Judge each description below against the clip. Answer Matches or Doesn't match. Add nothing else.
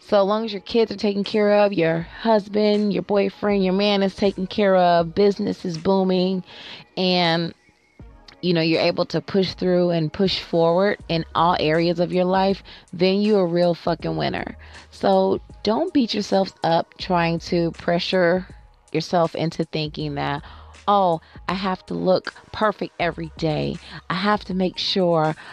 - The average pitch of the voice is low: Doesn't match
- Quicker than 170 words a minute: Doesn't match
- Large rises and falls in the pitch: Doesn't match